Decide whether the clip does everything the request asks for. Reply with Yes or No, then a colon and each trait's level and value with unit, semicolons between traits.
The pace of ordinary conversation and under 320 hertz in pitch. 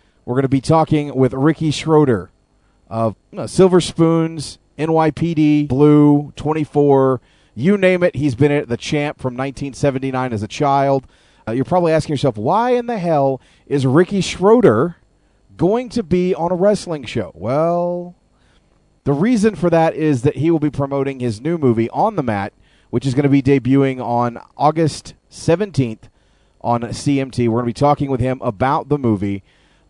Yes: average, 170 wpm; medium, 140 Hz